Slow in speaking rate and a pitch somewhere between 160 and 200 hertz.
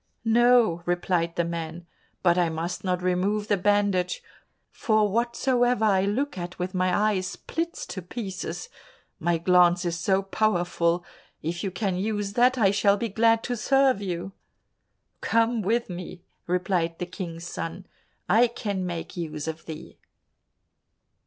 No: average, 145 wpm; high, 190 Hz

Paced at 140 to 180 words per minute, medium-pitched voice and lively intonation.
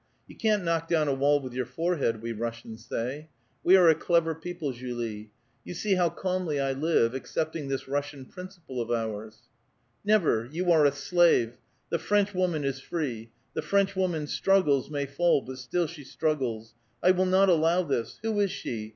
No: average, 190 wpm; medium, 150 Hz; wide, 5.8 semitones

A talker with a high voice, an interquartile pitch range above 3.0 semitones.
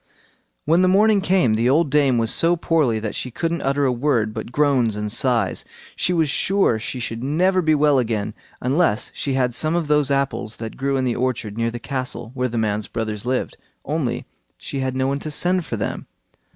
No: low, 130 Hz; average, 4.8 semitones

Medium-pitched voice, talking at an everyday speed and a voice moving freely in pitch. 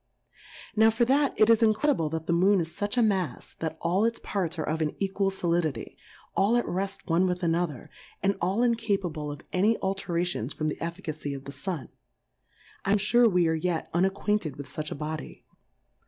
No: medium, 180 Hz; average, 190 wpm; average, 4.3 semitones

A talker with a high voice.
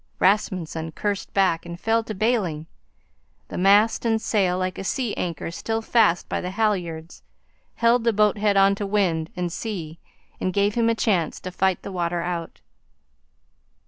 Yes: high, 195 Hz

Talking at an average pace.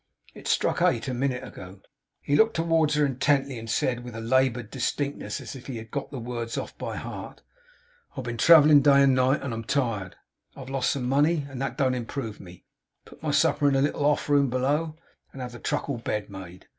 No: fast, 220 wpm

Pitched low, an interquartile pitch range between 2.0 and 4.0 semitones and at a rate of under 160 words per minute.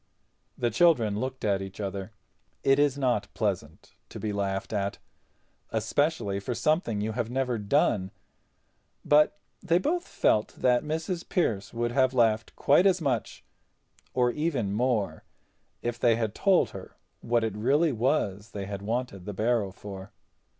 No: low, 115 Hz; average, 5.1 semitones; average, 150 wpm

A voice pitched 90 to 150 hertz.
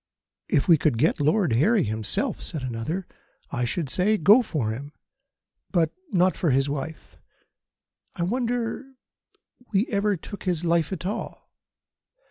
No: medium, 170 Hz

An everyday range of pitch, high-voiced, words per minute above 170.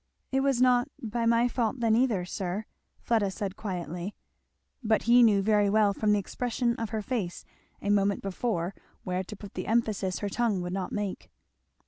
Yes: average, 3.3 semitones; high, 210 Hz; average, 180 wpm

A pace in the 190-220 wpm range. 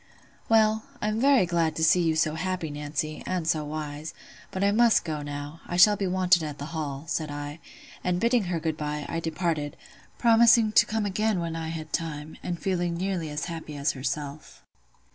Yes: average, 195 wpm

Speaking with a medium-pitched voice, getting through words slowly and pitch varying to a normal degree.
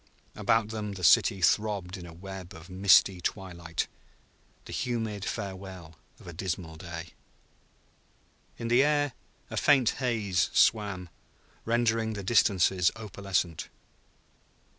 No: very low, 95 Hz; slow, 120 wpm; average, 3.7 semitones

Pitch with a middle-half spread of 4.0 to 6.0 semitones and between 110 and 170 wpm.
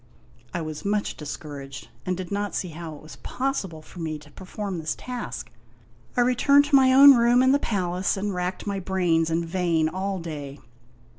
No: average, 4.7 semitones; average, 190 wpm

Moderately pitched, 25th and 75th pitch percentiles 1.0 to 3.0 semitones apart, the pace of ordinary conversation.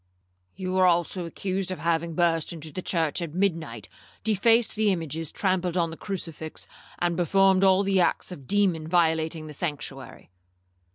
Yes: medium, 175 Hz; average, 2.7 semitones; average, 165 wpm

